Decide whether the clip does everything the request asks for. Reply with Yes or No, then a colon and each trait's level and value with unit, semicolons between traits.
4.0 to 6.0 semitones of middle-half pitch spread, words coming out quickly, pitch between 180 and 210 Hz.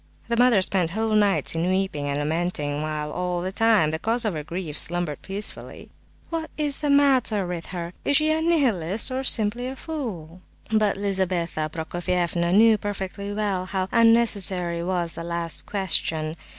No: average, 4.8 semitones; average, 165 wpm; high, 190 Hz